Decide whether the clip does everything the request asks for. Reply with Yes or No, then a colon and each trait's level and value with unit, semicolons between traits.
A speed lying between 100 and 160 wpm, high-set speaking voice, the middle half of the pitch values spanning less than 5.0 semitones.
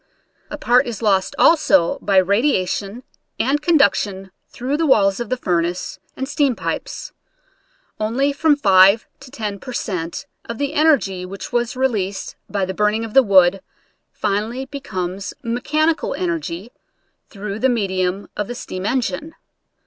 No: average, 150 wpm; high, 215 Hz; wide, 5.6 semitones